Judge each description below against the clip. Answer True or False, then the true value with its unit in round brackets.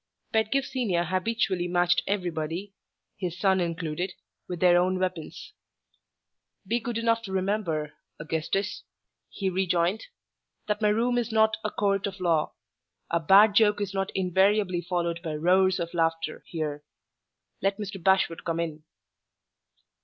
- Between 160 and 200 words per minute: False (140 wpm)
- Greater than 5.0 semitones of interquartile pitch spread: False (3.3 semitones)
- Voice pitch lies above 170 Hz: True (185 Hz)